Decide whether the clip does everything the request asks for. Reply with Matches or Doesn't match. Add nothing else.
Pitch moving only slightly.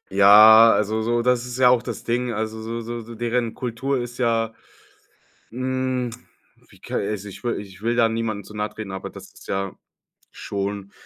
Matches